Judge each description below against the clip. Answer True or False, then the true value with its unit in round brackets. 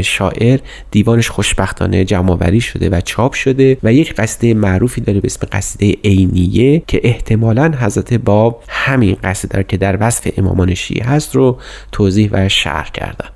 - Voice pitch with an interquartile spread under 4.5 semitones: True (4.0 semitones)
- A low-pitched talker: True (105 Hz)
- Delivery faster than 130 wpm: True (155 wpm)